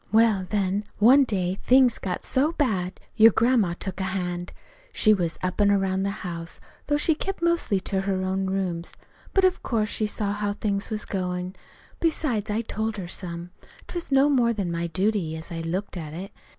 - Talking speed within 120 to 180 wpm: No, average, 195 wpm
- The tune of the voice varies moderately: Yes, average, 3.8 semitones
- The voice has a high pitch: Yes, high, 200 Hz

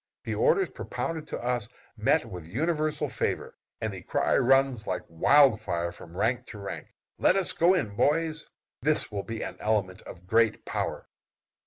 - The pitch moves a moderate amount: No, wide, 7.3 semitones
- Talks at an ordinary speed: Yes, average, 170 wpm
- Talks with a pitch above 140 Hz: No, low, 120 Hz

